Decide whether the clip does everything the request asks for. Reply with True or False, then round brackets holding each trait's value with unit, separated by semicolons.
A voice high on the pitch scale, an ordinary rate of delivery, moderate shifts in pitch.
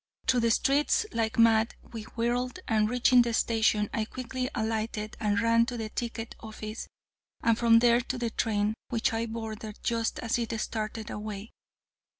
False (230 Hz; 165 wpm; 1.4 semitones)